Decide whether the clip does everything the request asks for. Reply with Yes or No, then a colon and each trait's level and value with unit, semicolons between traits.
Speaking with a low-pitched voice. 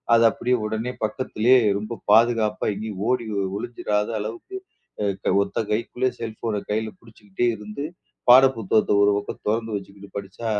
Yes: low, 110 Hz